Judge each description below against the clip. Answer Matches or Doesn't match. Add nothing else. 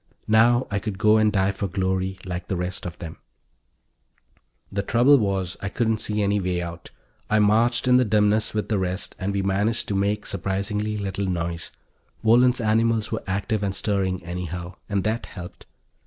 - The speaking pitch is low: Matches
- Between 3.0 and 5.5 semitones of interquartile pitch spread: Doesn't match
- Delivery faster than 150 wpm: Matches